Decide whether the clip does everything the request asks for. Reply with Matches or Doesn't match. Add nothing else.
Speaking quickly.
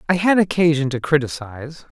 Doesn't match